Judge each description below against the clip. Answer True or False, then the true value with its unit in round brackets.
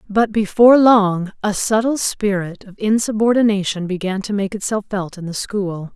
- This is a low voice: False (205 Hz)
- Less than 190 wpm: True (160 wpm)